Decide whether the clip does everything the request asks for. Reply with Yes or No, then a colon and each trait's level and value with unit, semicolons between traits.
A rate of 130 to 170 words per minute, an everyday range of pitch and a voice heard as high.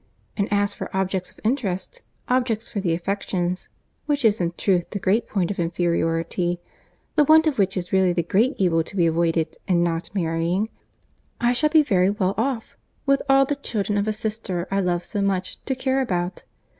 No: average, 195 wpm; average, 4.6 semitones; high, 195 Hz